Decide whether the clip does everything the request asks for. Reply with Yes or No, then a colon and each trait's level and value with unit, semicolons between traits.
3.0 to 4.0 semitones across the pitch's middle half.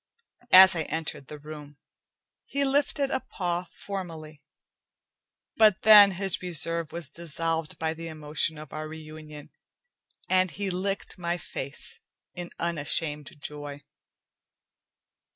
Yes: average, 3.3 semitones